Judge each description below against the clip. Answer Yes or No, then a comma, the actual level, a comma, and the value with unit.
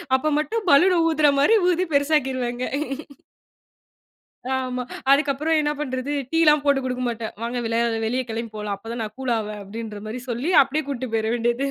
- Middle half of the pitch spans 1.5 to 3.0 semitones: No, average, 4.1 semitones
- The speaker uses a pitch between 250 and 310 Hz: Yes, very high, 255 Hz